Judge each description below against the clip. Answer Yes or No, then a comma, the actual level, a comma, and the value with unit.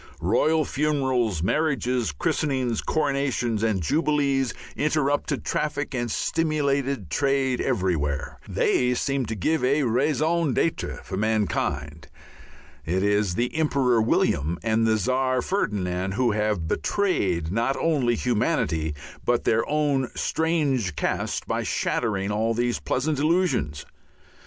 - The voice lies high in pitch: No, low, 125 Hz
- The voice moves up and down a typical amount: No, wide, 5.7 semitones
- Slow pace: Yes, slow, 120 wpm